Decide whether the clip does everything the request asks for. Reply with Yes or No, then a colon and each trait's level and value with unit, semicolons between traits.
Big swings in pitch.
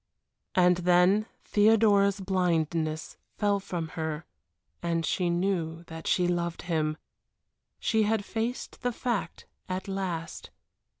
No: average, 3.3 semitones